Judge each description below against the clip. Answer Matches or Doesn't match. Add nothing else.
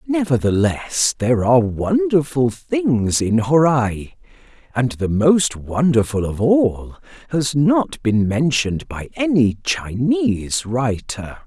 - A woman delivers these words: Doesn't match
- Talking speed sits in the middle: Doesn't match